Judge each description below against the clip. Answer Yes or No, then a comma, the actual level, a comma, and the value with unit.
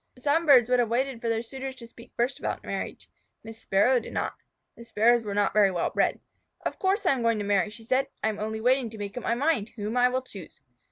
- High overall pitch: Yes, high, 235 Hz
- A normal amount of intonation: Yes, average, 3.3 semitones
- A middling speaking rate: No, fast, 255 wpm